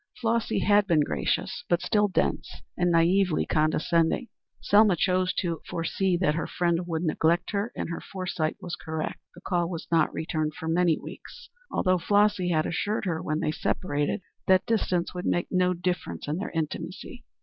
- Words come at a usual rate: Yes, average, 170 wpm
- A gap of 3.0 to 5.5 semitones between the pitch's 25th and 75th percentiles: No, narrow, 2.6 semitones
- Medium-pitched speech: Yes, medium, 175 Hz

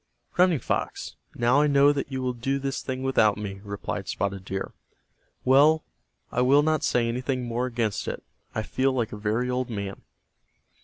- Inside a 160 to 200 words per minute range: Yes, average, 175 wpm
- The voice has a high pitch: No, low, 125 Hz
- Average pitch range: Yes, average, 3.9 semitones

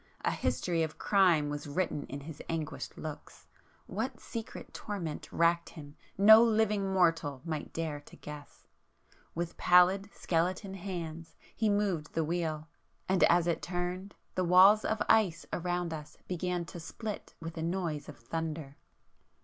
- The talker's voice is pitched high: No, medium, 170 Hz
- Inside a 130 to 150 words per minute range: Yes, average, 145 wpm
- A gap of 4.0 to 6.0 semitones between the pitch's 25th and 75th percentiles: No, average, 3.1 semitones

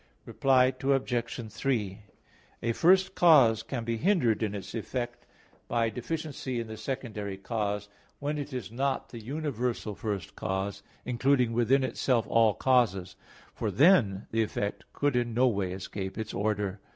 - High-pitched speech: No, low, 115 Hz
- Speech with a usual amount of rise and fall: Yes, average, 4.1 semitones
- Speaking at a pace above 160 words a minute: No, average, 150 wpm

